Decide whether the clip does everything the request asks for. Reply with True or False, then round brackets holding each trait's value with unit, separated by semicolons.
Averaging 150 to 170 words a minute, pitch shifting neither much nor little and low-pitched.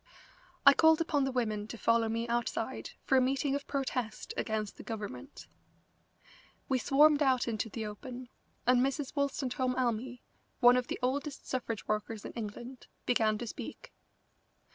False (155 wpm; 3.2 semitones; 245 Hz)